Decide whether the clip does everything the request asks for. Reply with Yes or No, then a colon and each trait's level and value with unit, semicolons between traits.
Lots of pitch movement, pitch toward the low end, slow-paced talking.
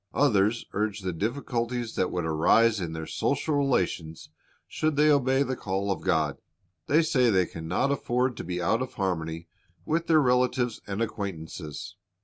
No: wide, 6.5 semitones; low, 110 Hz; average, 170 wpm